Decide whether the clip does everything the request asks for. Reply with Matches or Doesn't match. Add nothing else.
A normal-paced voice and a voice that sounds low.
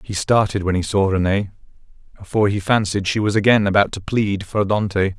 Matches